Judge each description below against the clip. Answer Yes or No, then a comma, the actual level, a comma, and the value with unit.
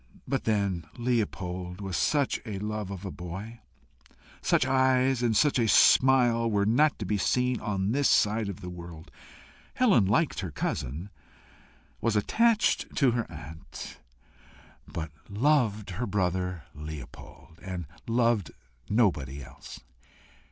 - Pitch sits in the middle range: No, low, 105 Hz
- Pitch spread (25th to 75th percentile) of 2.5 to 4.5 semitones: No, wide, 5.4 semitones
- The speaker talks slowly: Yes, slow, 130 wpm